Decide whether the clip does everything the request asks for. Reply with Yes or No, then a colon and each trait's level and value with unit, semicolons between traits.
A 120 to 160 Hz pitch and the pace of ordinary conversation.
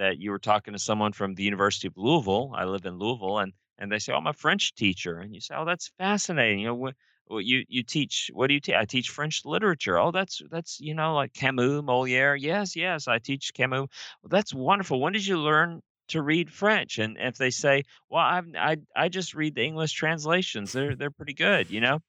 No: medium, 140 Hz; fast, 235 wpm